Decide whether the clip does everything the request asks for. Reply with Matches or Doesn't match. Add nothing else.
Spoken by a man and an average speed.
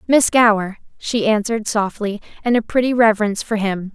Doesn't match